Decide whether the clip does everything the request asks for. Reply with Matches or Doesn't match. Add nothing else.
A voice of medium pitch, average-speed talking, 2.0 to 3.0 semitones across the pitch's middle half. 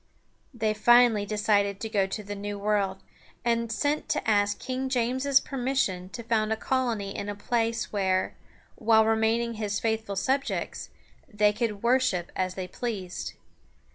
Doesn't match